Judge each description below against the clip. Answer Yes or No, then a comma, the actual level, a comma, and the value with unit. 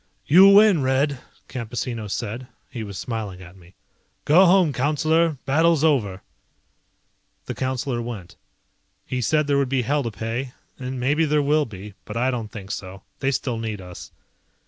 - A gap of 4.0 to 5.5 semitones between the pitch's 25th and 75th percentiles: Yes, average, 5.2 semitones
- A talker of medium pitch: No, low, 130 Hz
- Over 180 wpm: No, average, 165 wpm